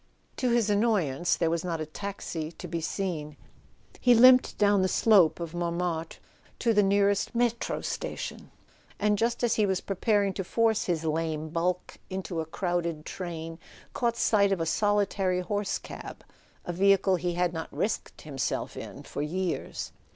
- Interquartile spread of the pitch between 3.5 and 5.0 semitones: Yes, average, 3.8 semitones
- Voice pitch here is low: No, medium, 185 Hz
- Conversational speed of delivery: Yes, average, 165 wpm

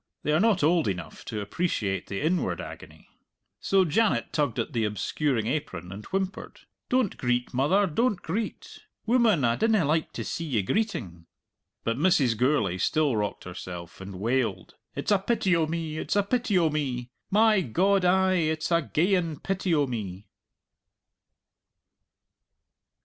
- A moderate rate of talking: Yes, average, 155 wpm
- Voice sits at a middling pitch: Yes, medium, 155 Hz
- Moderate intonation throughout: No, wide, 8.7 semitones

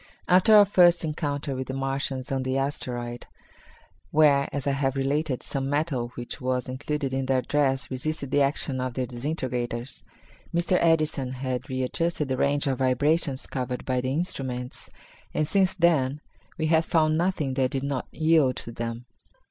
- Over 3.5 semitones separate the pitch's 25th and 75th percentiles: No, average, 3.2 semitones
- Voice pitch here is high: No, low, 135 Hz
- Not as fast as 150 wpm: No, average, 165 wpm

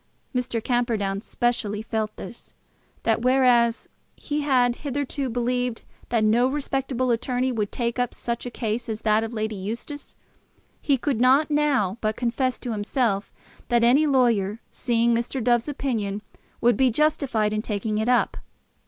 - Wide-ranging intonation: No, average, 2.8 semitones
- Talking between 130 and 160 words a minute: Yes, average, 155 wpm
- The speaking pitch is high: Yes, high, 240 Hz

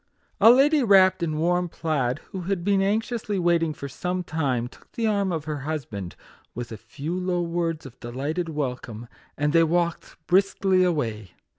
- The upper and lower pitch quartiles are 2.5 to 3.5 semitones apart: No, average, 4.8 semitones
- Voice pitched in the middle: Yes, medium, 165 Hz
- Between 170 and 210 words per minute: Yes, average, 175 wpm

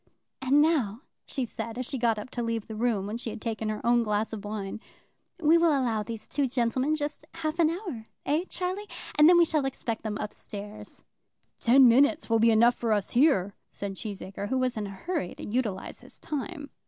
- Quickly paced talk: Yes, fast, 215 wpm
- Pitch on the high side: Yes, high, 235 Hz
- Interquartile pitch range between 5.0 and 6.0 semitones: Yes, average, 5.3 semitones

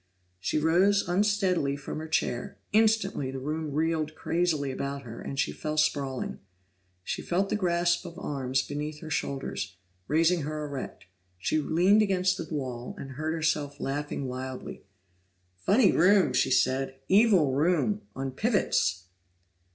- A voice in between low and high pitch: Yes, medium, 155 Hz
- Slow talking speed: No, average, 145 wpm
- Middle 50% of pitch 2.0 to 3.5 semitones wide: No, average, 4.8 semitones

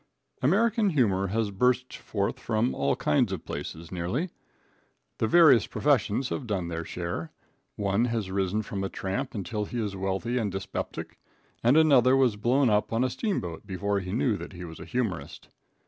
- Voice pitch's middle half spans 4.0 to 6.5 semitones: Yes, average, 4.8 semitones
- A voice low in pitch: Yes, low, 105 Hz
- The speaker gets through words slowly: No, average, 175 wpm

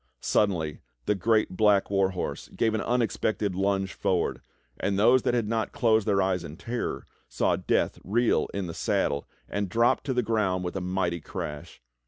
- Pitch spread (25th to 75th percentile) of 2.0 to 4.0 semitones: Yes, average, 3.3 semitones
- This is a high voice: No, low, 100 Hz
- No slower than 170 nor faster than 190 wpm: Yes, average, 180 wpm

